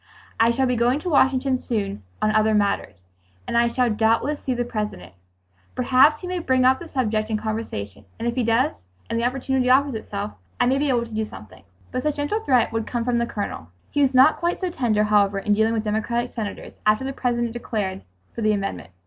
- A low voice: No, high, 235 Hz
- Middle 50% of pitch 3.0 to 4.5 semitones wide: Yes, average, 3.4 semitones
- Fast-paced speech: Yes, fast, 220 wpm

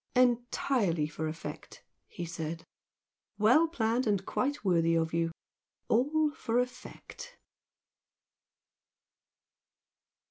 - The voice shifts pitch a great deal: Yes, wide, 7.3 semitones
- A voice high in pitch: Yes, high, 215 Hz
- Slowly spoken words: Yes, slow, 85 wpm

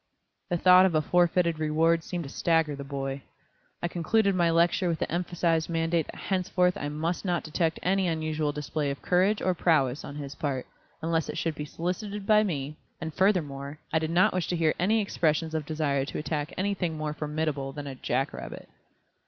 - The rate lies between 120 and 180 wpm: No, average, 195 wpm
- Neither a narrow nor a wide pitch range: Yes, average, 3.1 semitones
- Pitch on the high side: No, medium, 165 Hz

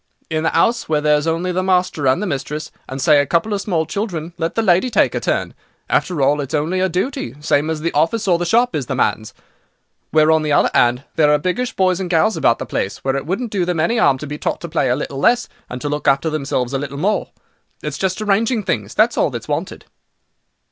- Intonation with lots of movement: No, average, 4.4 semitones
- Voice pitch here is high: No, medium, 160 Hz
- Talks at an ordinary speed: No, fast, 245 wpm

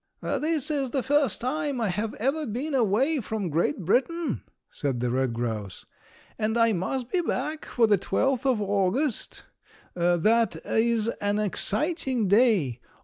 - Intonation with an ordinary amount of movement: No, wide, 6.0 semitones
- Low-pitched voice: No, high, 225 Hz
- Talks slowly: No, average, 145 wpm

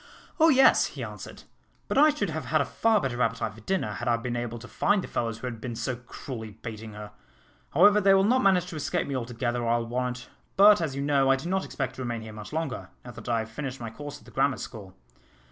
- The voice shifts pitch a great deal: Yes, wide, 5.7 semitones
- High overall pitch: No, low, 125 Hz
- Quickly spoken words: Yes, fast, 250 wpm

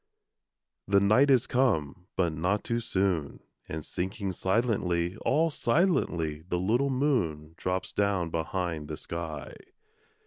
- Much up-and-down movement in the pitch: Yes, wide, 6.0 semitones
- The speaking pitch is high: No, very low, 95 Hz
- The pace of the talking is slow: Yes, slow, 125 wpm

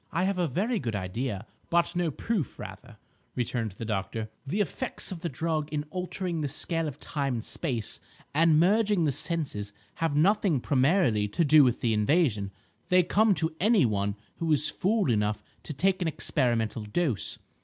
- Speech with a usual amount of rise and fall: No, wide, 7.5 semitones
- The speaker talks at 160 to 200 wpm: Yes, average, 175 wpm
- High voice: No, medium, 150 Hz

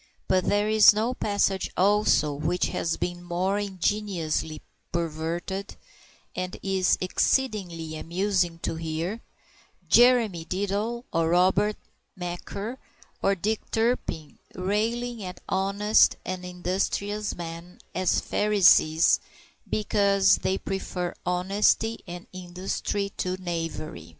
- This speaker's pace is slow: Yes, slow, 105 wpm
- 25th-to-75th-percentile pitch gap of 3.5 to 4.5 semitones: No, average, 3.0 semitones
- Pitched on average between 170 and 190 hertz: Yes, medium, 185 Hz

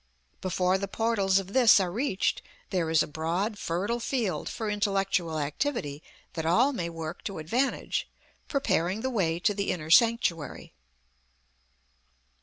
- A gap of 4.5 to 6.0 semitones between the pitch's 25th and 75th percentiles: Yes, average, 5.2 semitones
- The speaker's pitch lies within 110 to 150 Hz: No, high, 190 Hz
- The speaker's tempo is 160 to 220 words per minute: No, average, 140 wpm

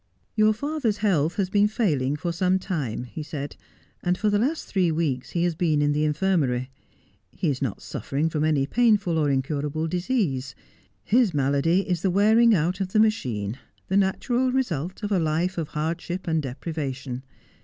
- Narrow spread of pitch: No, wide, 5.4 semitones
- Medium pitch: Yes, medium, 170 Hz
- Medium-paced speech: Yes, average, 175 wpm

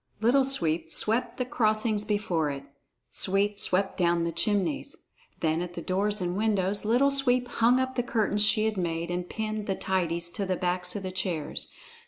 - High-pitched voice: Yes, high, 200 Hz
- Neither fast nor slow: Yes, average, 185 wpm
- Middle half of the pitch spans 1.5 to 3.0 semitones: No, average, 3.8 semitones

